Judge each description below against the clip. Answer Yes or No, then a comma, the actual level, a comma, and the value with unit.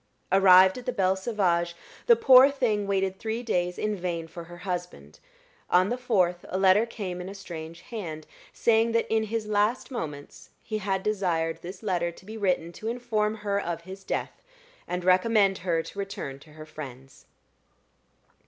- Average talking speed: Yes, average, 175 wpm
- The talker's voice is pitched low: No, high, 190 Hz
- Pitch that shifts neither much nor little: Yes, average, 3.8 semitones